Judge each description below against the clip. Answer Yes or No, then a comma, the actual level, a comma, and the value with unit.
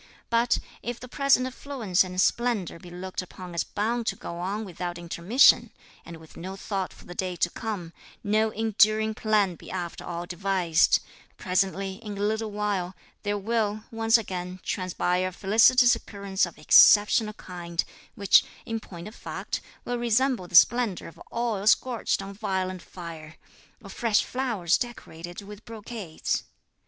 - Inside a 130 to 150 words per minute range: No, average, 160 wpm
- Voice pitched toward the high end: Yes, high, 200 Hz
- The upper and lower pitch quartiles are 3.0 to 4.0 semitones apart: Yes, average, 3.7 semitones